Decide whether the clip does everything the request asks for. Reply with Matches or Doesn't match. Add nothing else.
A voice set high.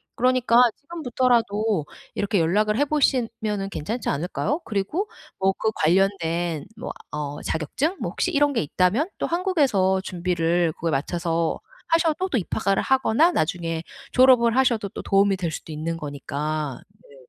Matches